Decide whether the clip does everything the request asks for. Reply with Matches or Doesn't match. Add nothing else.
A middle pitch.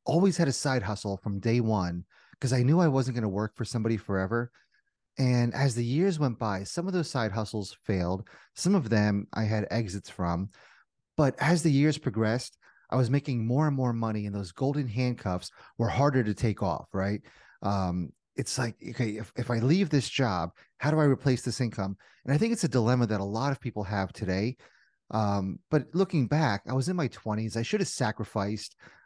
Doesn't match